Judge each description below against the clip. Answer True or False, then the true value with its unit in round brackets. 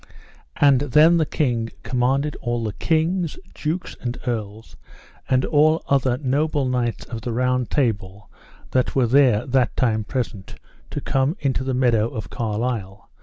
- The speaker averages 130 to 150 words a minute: True (145 wpm)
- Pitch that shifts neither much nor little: True (3.8 semitones)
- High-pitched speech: False (125 Hz)